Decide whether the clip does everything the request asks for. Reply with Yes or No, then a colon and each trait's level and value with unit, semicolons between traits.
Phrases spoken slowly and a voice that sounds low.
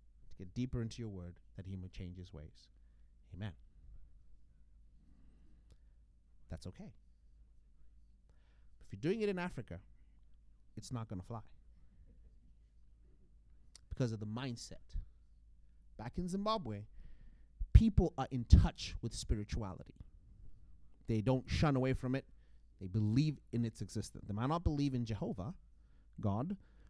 Yes: slow, 125 wpm; very low, 95 Hz